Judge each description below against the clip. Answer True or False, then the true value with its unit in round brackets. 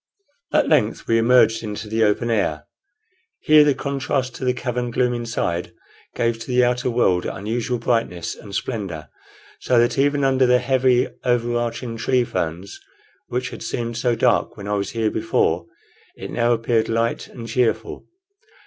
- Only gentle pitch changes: True (2.0 semitones)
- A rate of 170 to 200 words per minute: False (160 wpm)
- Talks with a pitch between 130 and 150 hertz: False (120 Hz)